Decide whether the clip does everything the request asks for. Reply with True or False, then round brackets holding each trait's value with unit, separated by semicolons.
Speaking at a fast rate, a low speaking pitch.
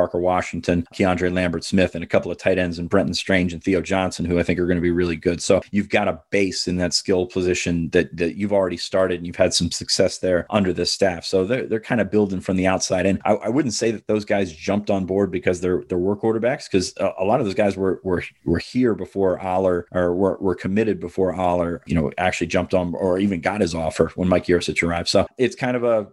True (255 wpm; 90 Hz)